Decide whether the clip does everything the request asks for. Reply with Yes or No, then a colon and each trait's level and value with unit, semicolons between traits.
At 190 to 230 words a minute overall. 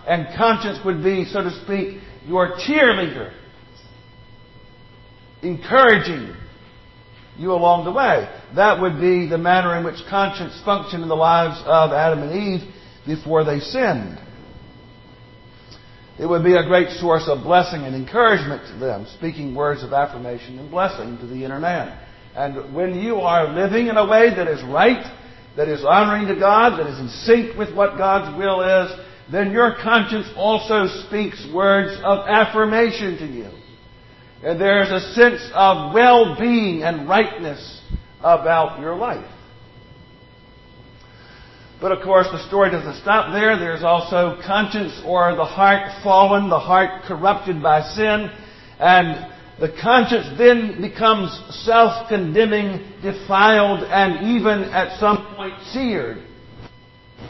No: average, 140 wpm